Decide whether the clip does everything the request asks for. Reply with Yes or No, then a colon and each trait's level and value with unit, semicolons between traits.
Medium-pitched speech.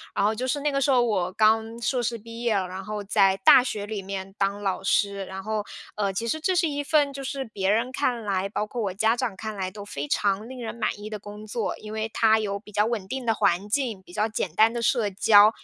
No: high, 215 Hz